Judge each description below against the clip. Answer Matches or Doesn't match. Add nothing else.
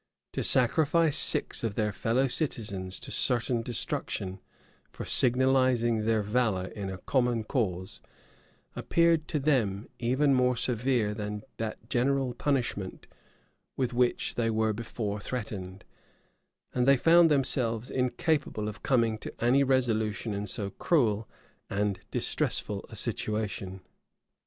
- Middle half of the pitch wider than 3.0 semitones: Matches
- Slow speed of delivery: Matches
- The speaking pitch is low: Matches